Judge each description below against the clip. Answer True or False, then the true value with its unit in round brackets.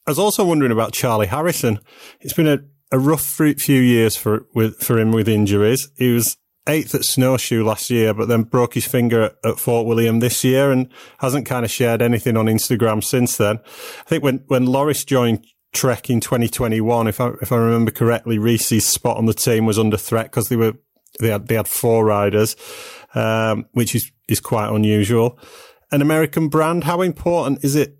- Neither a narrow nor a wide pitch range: True (3.3 semitones)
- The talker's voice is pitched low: True (120 Hz)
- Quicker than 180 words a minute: True (200 wpm)